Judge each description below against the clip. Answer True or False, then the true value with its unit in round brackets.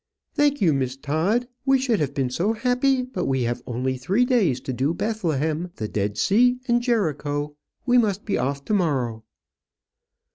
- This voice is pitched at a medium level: True (165 Hz)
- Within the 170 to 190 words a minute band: True (175 wpm)